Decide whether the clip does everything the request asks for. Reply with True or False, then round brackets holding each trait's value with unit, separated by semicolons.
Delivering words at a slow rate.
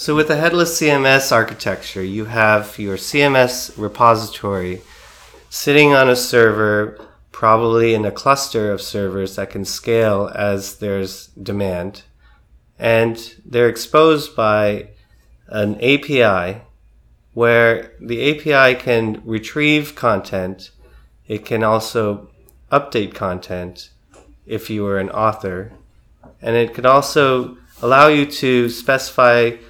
True (115 wpm)